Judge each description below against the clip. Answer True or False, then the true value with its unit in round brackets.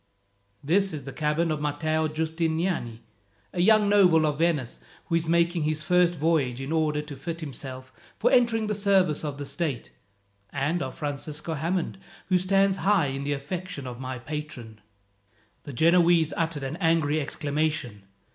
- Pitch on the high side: False (155 Hz)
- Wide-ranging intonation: False (3.3 semitones)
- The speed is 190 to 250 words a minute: False (160 wpm)